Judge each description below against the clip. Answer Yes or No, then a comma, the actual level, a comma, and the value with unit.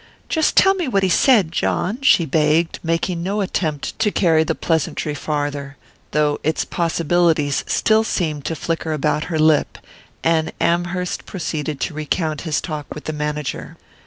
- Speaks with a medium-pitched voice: Yes, medium, 160 Hz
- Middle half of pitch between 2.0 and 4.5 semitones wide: Yes, average, 2.7 semitones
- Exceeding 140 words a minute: Yes, average, 160 wpm